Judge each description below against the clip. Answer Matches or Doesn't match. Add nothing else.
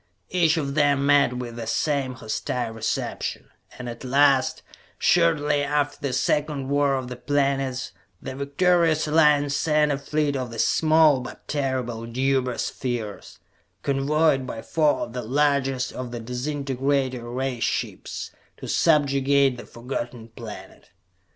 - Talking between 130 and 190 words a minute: Matches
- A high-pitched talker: Doesn't match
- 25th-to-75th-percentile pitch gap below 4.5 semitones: Matches